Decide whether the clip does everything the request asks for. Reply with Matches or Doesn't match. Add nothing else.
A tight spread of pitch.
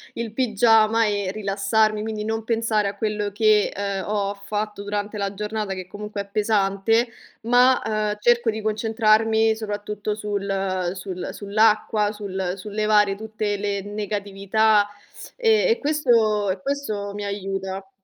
Matches